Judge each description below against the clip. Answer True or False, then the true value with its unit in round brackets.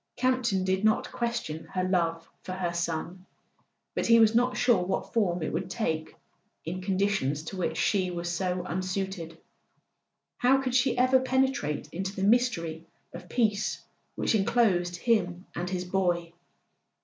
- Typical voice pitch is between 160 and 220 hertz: True (185 Hz)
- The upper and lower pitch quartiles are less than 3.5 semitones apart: False (4.8 semitones)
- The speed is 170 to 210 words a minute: False (150 wpm)